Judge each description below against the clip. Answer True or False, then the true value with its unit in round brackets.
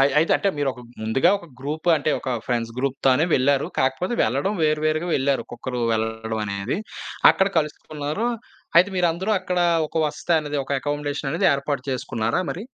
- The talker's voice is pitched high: False (145 Hz)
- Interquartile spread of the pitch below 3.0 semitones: False (3.7 semitones)